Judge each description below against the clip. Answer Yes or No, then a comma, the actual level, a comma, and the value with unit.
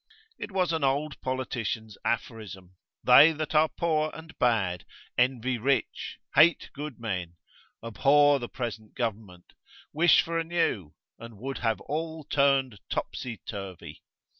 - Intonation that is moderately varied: No, wide, 5.7 semitones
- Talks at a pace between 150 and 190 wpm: No, slow, 135 wpm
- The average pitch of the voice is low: Yes, low, 130 Hz